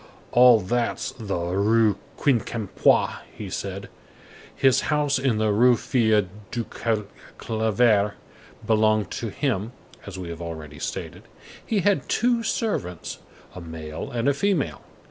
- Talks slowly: Yes, slow, 130 wpm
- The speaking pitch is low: Yes, low, 110 Hz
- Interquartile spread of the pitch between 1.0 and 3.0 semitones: No, average, 4.7 semitones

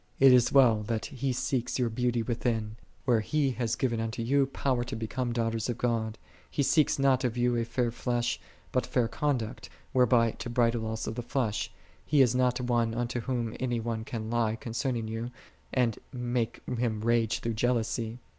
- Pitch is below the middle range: Yes, low, 120 Hz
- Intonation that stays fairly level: Yes, narrow, 1.8 semitones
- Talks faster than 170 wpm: Yes, average, 185 wpm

